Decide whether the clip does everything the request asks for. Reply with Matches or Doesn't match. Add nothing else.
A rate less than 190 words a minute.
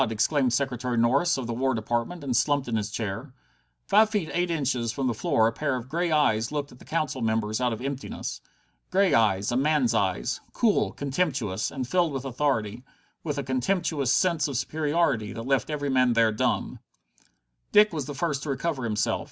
Doesn't match